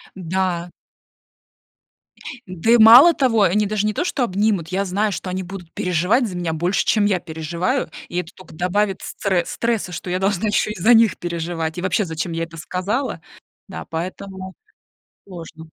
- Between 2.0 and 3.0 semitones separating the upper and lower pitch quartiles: No, average, 3.4 semitones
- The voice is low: No, medium, 185 Hz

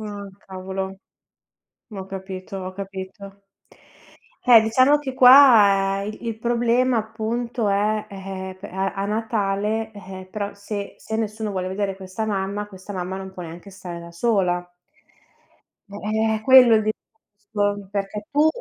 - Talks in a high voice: Yes, high, 205 Hz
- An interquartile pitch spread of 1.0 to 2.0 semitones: No, narrow, 2.4 semitones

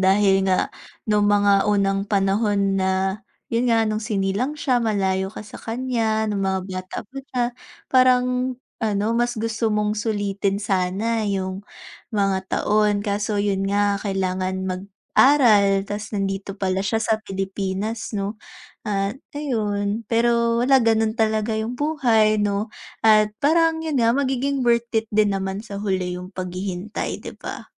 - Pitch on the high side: Yes, high, 210 Hz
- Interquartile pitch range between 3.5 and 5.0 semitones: No, average, 2.8 semitones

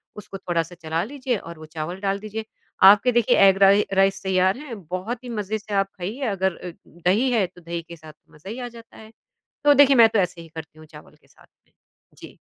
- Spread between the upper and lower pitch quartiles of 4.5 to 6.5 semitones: Yes, average, 4.8 semitones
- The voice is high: Yes, high, 195 Hz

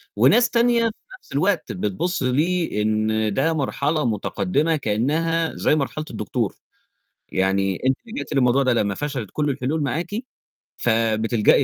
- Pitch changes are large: Yes, wide, 6.7 semitones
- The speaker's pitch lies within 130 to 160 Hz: Yes, low, 135 Hz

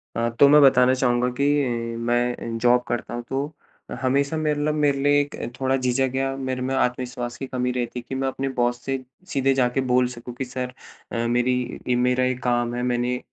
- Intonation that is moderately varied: No, narrow, 1.6 semitones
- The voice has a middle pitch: No, low, 125 Hz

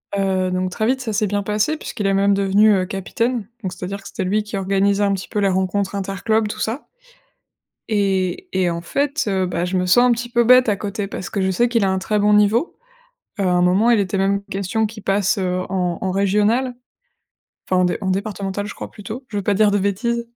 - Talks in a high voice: Yes, high, 200 Hz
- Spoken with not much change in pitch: Yes, narrow, 2.3 semitones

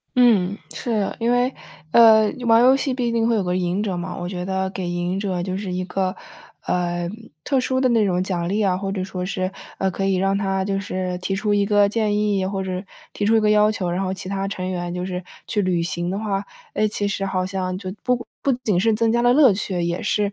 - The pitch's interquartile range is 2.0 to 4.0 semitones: Yes, average, 2.7 semitones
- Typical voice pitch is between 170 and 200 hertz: Yes, high, 195 Hz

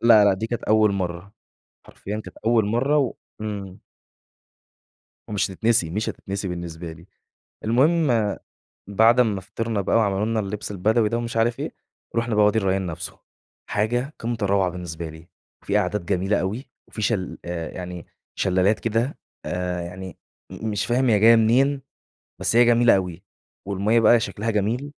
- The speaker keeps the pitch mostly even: No, average, 3.6 semitones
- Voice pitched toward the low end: Yes, low, 105 Hz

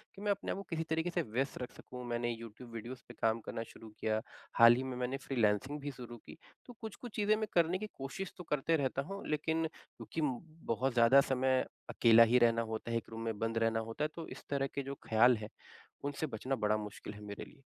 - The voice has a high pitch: No, low, 125 Hz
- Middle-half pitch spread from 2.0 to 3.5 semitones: No, average, 4.7 semitones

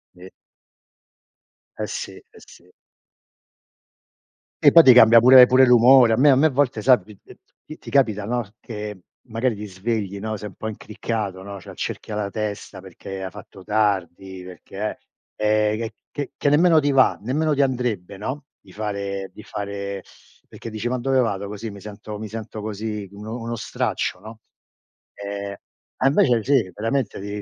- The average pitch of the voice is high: No, low, 110 Hz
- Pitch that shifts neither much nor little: Yes, average, 3.5 semitones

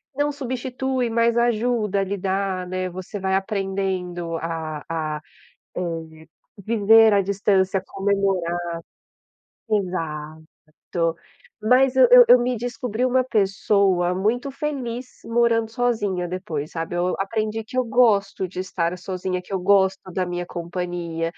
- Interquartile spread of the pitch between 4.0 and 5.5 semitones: Yes, average, 4.5 semitones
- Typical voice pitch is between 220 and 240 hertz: No, high, 195 Hz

